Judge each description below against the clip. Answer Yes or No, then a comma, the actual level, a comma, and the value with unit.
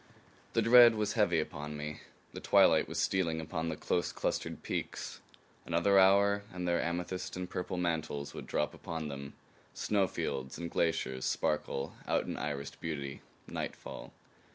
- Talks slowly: No, average, 150 wpm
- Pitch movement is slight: No, average, 3.8 semitones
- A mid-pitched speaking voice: No, very low, 85 Hz